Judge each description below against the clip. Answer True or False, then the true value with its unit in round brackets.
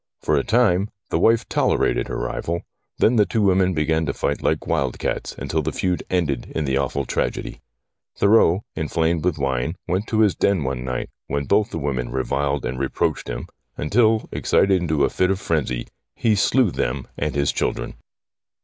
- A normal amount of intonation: False (6.0 semitones)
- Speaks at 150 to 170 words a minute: False (185 wpm)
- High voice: False (80 Hz)